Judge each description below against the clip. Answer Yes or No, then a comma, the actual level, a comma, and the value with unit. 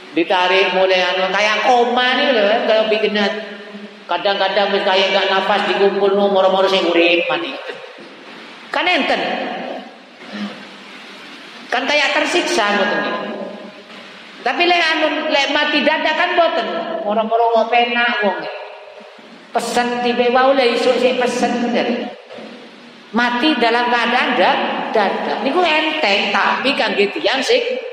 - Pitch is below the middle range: No, high, 240 Hz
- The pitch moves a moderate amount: No, wide, 5.7 semitones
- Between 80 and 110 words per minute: No, average, 135 wpm